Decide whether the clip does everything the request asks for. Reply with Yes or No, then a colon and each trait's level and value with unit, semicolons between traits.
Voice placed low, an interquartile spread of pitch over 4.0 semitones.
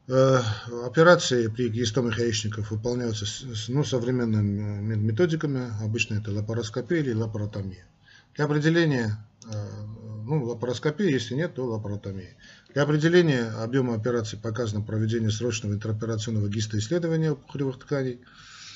No: low, 120 Hz; average, 3.6 semitones